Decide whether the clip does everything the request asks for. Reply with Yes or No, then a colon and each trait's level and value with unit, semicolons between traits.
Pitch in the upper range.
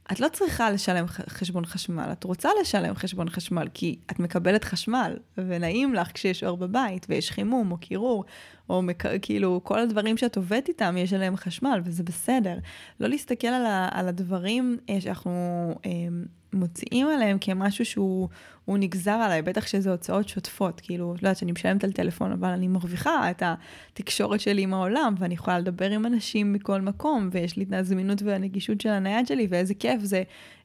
Yes: high, 195 Hz